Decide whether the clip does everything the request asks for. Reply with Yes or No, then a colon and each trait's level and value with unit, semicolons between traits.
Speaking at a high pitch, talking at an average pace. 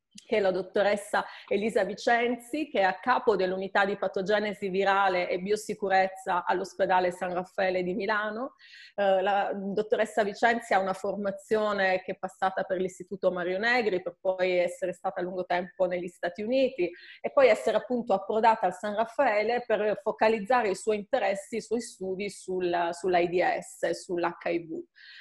Yes: high, 195 Hz; average, 150 wpm